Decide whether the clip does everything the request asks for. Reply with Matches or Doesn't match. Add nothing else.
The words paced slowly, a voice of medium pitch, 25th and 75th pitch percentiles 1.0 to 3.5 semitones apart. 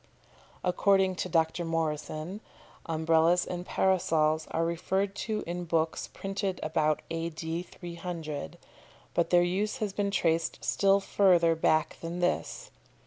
Matches